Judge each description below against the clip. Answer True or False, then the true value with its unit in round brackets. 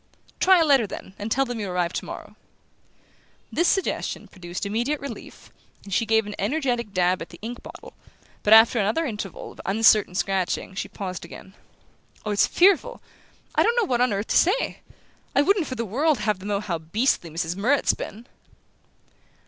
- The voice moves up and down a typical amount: False (5.9 semitones)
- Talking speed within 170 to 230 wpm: True (180 wpm)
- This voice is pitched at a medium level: False (220 Hz)